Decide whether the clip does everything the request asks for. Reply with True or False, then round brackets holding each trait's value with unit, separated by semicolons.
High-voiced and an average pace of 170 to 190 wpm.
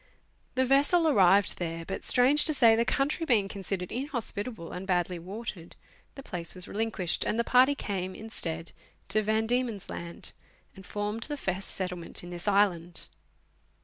False (205 Hz; 160 wpm)